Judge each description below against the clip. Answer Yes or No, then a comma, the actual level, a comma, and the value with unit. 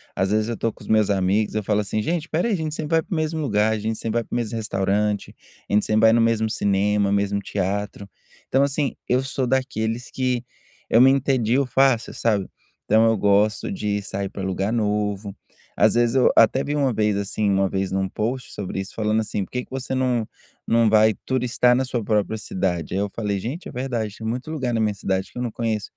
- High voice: No, low, 110 Hz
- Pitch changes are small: No, average, 3.6 semitones